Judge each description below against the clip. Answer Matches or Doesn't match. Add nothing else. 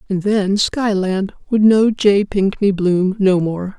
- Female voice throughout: Matches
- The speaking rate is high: Doesn't match